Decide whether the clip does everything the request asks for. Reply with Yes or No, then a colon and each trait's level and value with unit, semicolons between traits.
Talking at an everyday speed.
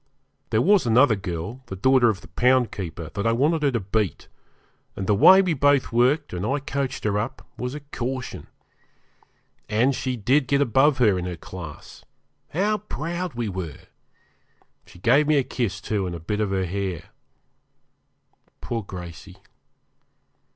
Yes: average, 165 wpm